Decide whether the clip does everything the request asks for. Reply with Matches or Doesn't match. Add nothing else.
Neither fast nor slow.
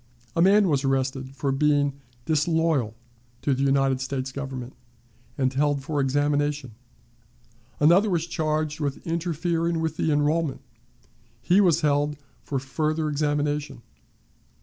Doesn't match